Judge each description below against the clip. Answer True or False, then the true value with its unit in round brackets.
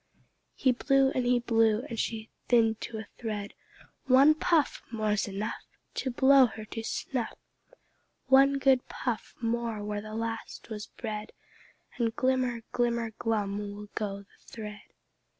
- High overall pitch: True (230 Hz)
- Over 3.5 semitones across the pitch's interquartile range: False (3.0 semitones)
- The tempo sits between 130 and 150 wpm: True (140 wpm)